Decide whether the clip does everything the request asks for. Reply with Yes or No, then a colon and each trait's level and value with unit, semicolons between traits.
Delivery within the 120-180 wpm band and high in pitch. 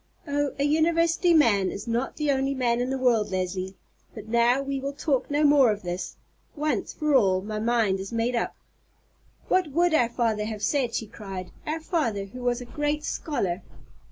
No: average, 190 wpm; high, 245 Hz